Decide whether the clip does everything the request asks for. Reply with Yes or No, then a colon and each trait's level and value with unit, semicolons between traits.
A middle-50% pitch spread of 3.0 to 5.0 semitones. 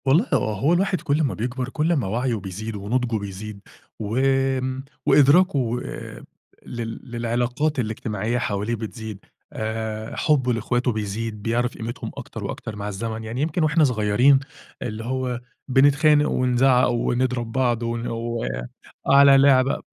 Yes: average, 3.3 semitones